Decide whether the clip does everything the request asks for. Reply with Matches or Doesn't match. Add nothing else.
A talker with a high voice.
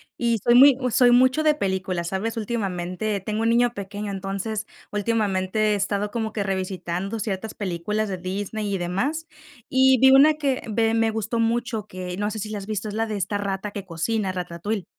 Matches